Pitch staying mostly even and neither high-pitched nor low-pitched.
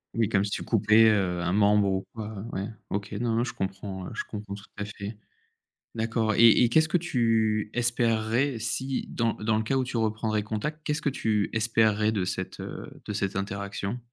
No: narrow, 2.2 semitones; low, 110 Hz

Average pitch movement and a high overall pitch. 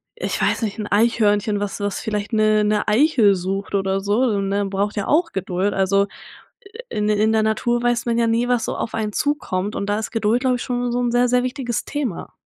Yes: average, 3.0 semitones; high, 215 Hz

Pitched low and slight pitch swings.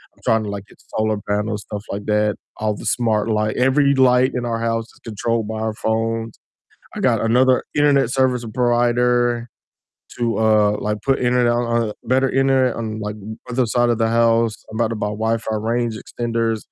Yes: low, 115 Hz; narrow, 2.0 semitones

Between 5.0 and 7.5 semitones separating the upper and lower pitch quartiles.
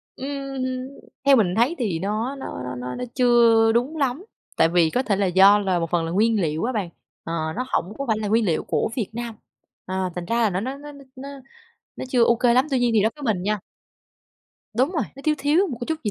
Yes: average, 5.3 semitones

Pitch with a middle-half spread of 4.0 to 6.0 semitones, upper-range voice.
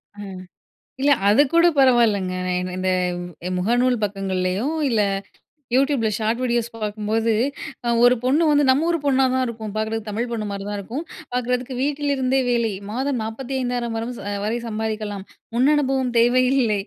No: average, 3.5 semitones; high, 235 Hz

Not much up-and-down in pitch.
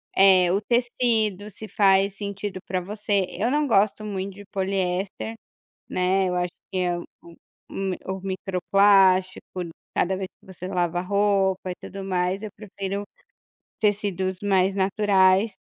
Yes: narrow, 1.6 semitones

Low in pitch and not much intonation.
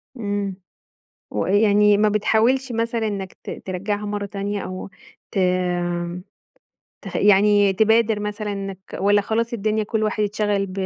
No: high, 205 Hz; narrow, 1.4 semitones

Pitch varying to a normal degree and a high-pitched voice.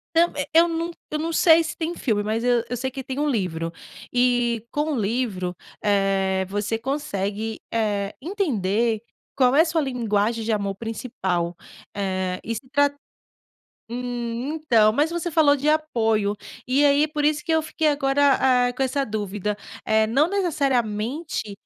No: wide, 5.8 semitones; high, 245 Hz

